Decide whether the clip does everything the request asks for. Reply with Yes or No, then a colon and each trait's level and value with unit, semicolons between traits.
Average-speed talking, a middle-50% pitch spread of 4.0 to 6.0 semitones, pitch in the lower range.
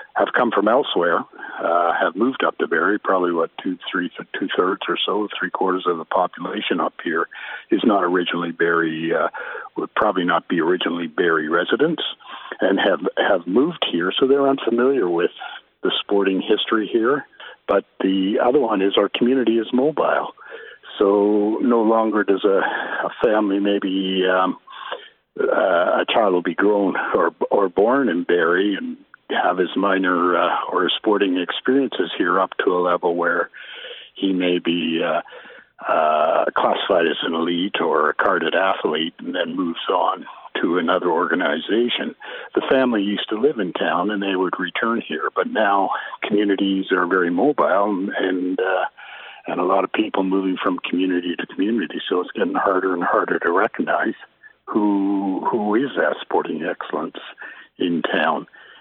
No: average, 160 wpm; average, 2.9 semitones; very low, 95 Hz